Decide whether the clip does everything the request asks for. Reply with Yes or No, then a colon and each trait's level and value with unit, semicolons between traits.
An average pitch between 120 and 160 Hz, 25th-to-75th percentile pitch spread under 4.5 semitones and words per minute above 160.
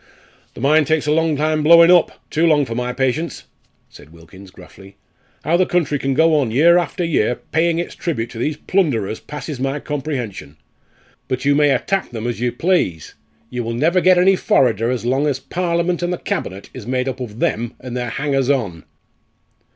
No: medium, 140 Hz; average, 5.3 semitones; average, 195 wpm